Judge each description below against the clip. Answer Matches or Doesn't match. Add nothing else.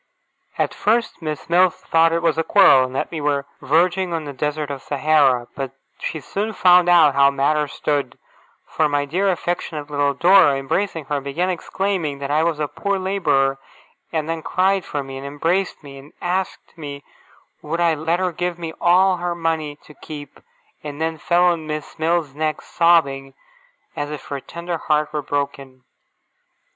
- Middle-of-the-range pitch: Matches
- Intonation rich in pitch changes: Doesn't match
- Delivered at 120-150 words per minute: Doesn't match